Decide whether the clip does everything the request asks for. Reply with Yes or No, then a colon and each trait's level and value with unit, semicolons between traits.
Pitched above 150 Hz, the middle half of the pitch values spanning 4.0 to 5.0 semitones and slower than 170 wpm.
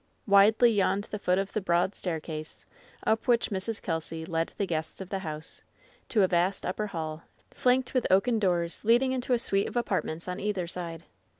No: high, 190 Hz; average, 4.4 semitones; average, 190 wpm